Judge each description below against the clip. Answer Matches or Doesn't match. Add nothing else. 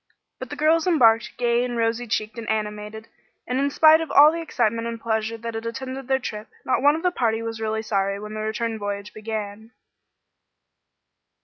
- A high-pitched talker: Matches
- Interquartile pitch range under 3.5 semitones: Matches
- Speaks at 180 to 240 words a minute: Matches